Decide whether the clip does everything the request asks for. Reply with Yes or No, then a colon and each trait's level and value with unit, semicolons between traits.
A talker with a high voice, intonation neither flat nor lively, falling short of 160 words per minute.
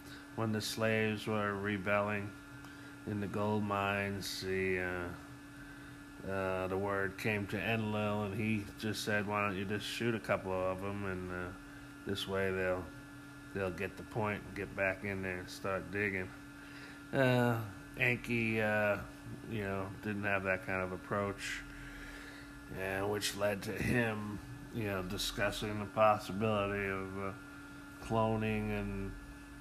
No: low, 105 Hz; average, 4.2 semitones; average, 145 wpm